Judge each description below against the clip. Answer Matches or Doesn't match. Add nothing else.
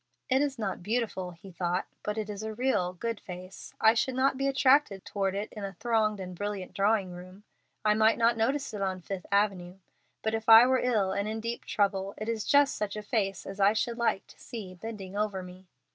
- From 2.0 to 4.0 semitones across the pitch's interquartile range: Matches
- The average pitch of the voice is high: Matches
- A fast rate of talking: Matches